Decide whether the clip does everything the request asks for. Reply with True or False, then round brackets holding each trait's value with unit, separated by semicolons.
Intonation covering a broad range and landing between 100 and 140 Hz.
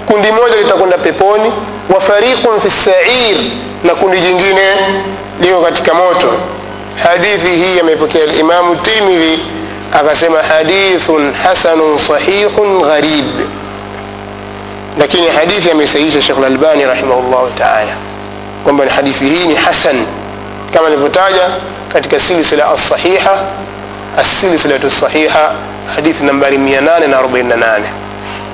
False (6.7 semitones; 160 Hz)